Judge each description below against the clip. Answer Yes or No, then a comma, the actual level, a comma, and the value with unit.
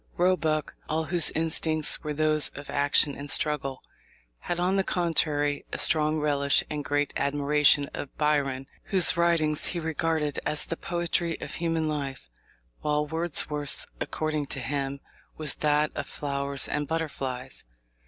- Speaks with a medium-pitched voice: Yes, medium, 150 Hz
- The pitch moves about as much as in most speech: No, narrow, 2.1 semitones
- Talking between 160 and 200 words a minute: No, average, 145 wpm